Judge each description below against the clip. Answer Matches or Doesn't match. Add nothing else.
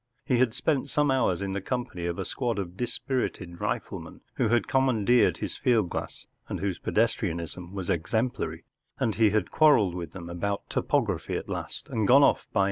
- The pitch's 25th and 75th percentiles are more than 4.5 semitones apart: Matches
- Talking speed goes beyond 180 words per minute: Matches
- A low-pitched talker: Matches